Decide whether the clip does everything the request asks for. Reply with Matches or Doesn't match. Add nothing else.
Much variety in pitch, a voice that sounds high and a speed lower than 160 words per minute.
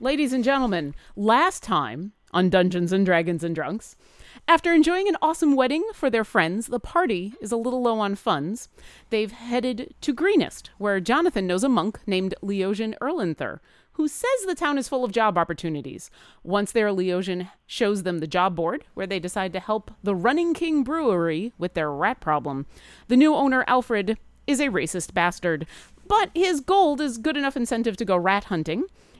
Doesn't match